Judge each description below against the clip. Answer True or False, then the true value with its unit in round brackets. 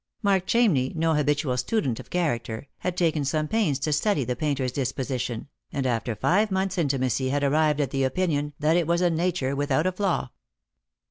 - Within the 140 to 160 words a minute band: False (185 wpm)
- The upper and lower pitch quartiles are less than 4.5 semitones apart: False (4.9 semitones)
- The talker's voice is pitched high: False (150 Hz)